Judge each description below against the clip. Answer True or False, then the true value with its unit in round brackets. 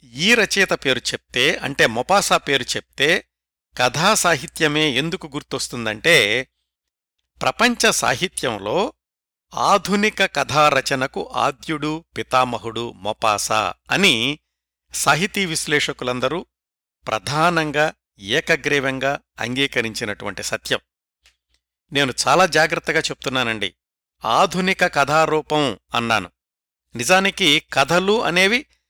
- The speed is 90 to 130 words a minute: False (75 wpm)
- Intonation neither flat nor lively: False (7.5 semitones)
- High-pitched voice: False (145 Hz)